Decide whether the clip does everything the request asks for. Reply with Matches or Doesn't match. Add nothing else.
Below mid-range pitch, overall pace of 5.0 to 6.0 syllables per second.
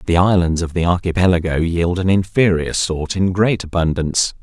Matches